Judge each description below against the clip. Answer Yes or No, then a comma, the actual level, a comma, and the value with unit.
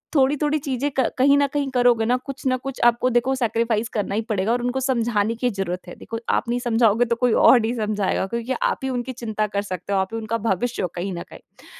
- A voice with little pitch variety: No, average, 3.1 semitones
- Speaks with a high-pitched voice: Yes, high, 235 Hz